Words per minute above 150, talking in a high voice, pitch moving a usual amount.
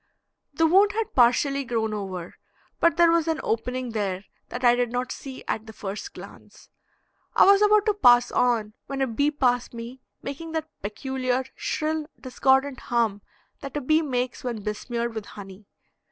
Yes: average, 170 wpm; very high, 250 Hz; average, 4.7 semitones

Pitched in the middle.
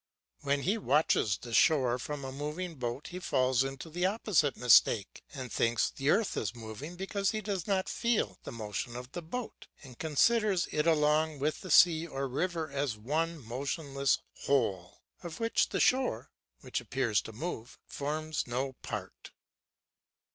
Yes: medium, 145 Hz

